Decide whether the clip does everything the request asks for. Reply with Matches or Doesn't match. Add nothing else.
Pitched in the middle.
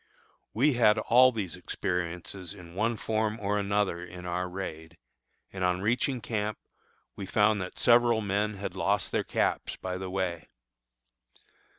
Doesn't match